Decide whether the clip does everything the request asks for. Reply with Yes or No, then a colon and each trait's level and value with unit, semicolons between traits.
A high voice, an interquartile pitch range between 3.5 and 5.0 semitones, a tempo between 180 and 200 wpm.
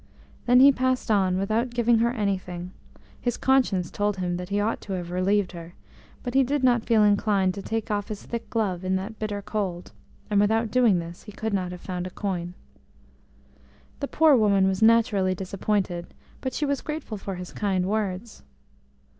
Yes: high, 205 Hz; average, 3.8 semitones; average, 190 wpm